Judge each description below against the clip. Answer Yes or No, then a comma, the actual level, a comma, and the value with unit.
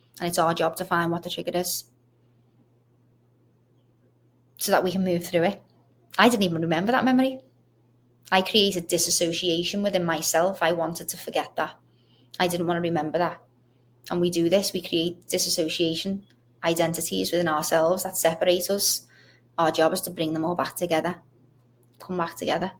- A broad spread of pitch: Yes, wide, 6.4 semitones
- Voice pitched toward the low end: No, medium, 165 Hz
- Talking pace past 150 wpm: Yes, fast, 170 wpm